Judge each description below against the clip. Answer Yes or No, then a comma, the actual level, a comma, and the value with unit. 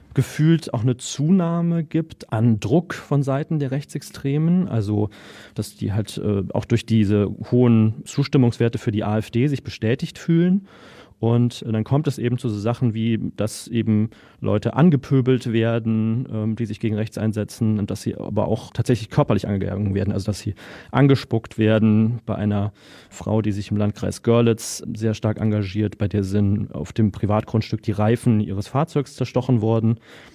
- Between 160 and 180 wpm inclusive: Yes, average, 165 wpm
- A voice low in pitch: Yes, low, 115 Hz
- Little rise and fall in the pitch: No, average, 3.4 semitones